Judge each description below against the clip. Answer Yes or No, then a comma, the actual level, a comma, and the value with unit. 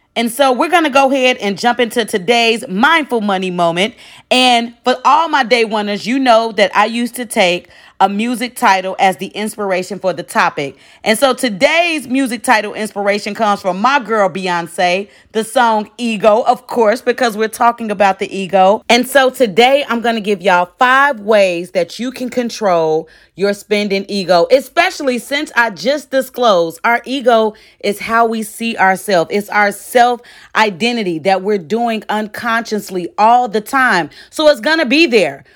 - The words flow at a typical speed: Yes, average, 170 wpm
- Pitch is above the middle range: Yes, high, 225 Hz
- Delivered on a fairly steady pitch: No, average, 3.8 semitones